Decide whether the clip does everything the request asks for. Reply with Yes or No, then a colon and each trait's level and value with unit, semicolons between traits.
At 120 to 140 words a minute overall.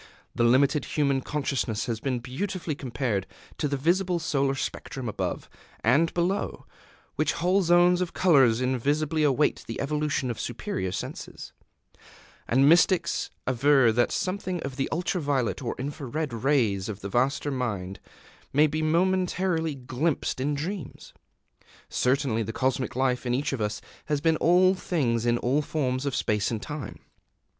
No: average, 150 wpm